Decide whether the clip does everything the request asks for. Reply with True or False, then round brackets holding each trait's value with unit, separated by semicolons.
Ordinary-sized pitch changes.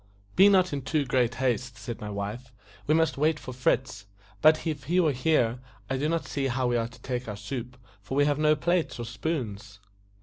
True (4.5 semitones)